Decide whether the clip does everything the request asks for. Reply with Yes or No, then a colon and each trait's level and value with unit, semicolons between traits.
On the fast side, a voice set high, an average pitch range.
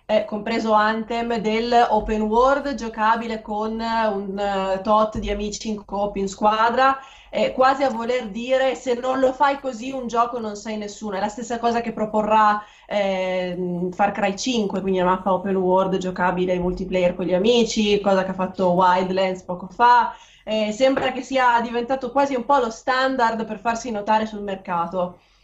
Yes: fast, 175 wpm; high, 215 Hz; average, 3.6 semitones